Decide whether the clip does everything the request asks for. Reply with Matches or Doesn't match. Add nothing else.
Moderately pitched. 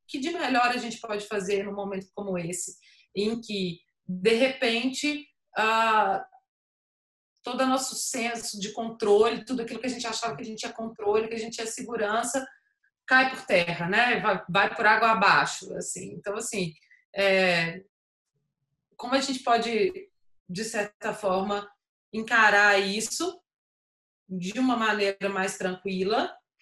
Doesn't match